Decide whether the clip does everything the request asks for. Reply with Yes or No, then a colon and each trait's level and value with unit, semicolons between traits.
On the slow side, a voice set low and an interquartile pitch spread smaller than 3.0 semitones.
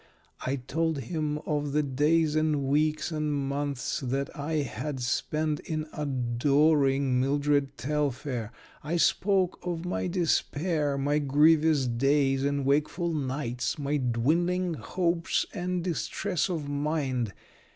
No: slow, 120 wpm; medium, 150 Hz; narrow, 2.6 semitones